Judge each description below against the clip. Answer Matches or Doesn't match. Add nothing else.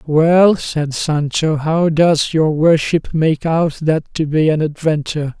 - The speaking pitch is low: Doesn't match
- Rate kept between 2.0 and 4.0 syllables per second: Matches